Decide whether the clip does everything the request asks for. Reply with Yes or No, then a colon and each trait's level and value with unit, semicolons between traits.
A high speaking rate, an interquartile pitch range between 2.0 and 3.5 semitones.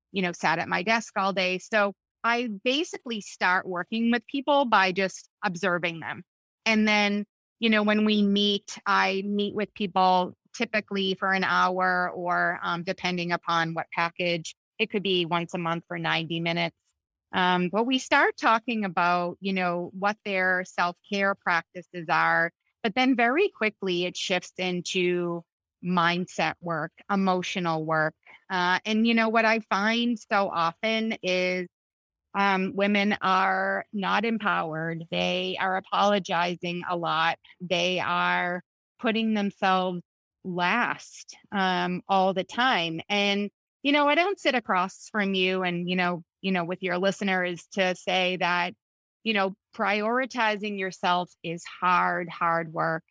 No: average, 150 wpm; average, 2.9 semitones